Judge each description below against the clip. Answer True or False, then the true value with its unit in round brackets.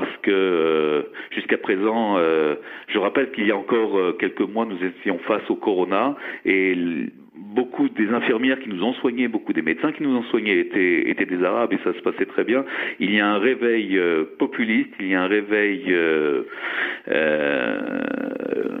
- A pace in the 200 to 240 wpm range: False (175 wpm)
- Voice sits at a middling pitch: False (115 Hz)